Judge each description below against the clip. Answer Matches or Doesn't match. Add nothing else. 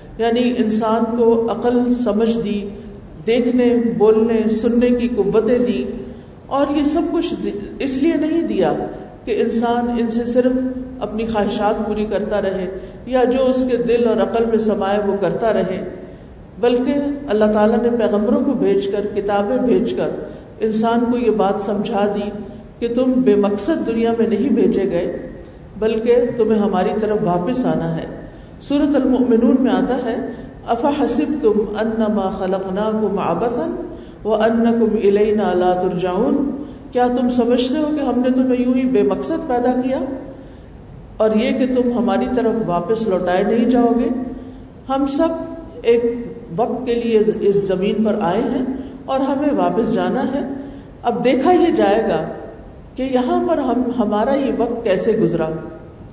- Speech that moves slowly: Doesn't match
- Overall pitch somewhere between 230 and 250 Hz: Matches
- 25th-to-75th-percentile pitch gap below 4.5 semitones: Matches